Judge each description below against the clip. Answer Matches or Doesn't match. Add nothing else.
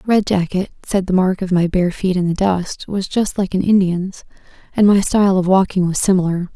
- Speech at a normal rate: Doesn't match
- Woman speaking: Matches